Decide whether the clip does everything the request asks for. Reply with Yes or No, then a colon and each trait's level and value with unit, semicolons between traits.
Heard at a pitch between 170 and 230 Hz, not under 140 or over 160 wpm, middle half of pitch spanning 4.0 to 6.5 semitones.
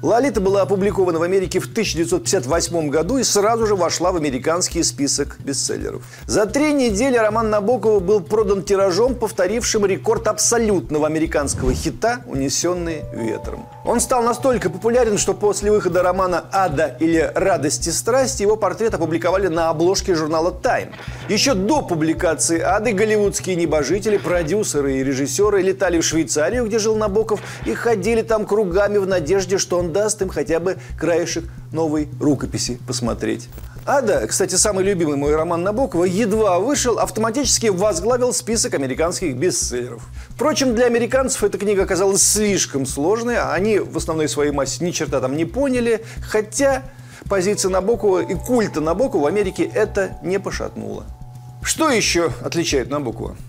Yes: medium, 185 Hz; average, 145 wpm; average, 5.3 semitones